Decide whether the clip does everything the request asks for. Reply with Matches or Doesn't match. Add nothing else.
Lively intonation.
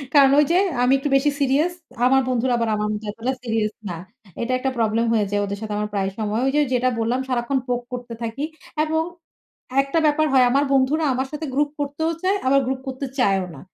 Doesn't match